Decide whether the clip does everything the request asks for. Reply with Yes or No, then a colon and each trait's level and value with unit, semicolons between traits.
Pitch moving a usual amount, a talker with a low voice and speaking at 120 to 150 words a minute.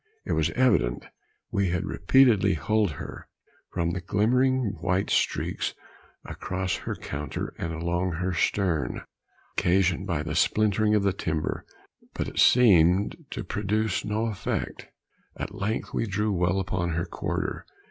Yes: average, 3.6 semitones; very low, 95 Hz; average, 140 wpm